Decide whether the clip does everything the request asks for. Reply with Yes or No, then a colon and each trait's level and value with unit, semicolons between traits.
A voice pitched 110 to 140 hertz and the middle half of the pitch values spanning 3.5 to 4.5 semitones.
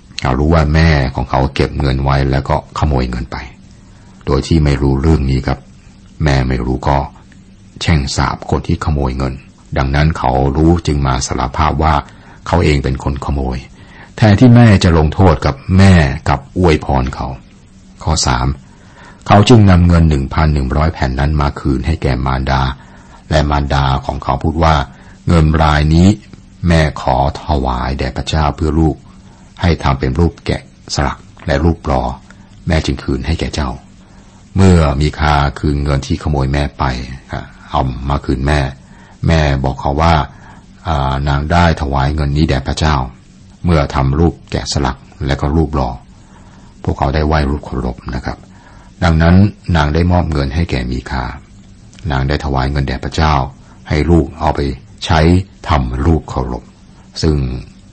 No: very low, 75 Hz; average, 4.1 semitones